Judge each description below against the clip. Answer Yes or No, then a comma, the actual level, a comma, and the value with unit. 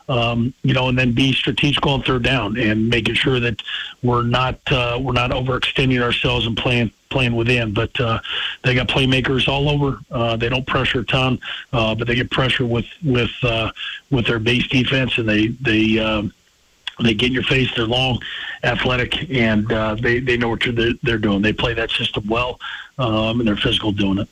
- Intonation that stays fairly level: Yes, narrow, 2.2 semitones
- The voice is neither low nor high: No, low, 120 Hz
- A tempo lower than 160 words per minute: No, average, 200 wpm